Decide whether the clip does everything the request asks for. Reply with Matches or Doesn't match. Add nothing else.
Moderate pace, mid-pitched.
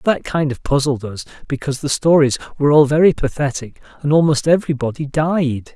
Matches